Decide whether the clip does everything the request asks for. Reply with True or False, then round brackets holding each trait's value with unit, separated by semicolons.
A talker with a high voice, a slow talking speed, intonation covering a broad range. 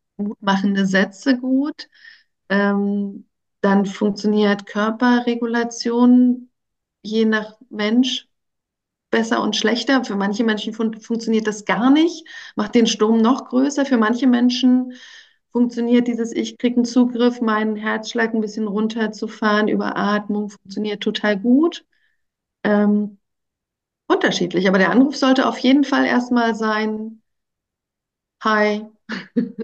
False (225 Hz; 115 wpm; 2.9 semitones)